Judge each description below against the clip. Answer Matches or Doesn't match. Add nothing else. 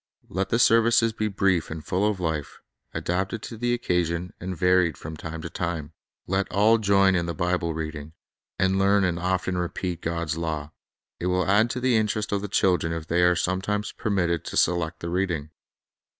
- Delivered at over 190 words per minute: Matches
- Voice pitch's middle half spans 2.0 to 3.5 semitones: Matches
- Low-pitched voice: Matches